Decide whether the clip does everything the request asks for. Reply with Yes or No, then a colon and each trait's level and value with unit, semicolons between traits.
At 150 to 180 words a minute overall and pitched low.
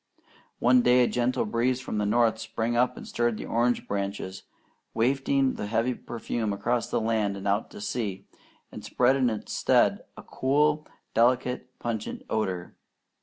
Yes: average, 165 wpm; low, 120 Hz